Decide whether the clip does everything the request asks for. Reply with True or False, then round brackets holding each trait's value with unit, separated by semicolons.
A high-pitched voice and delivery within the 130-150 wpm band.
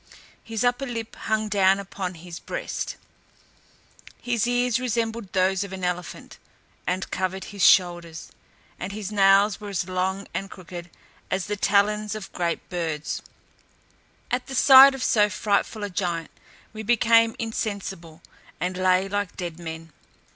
True (195 Hz; 145 wpm)